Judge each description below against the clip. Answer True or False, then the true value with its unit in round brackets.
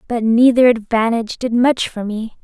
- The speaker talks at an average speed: True (170 wpm)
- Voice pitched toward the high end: True (230 Hz)